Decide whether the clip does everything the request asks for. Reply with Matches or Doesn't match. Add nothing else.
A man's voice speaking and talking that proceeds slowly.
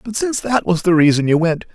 Doesn't match